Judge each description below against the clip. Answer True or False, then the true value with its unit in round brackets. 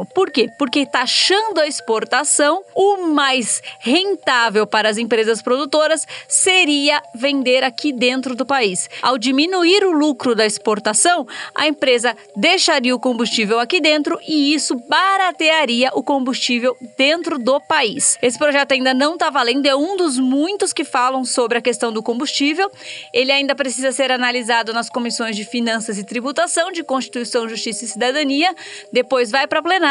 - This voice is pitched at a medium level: False (270 Hz)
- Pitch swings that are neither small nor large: True (4.2 semitones)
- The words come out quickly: False (155 wpm)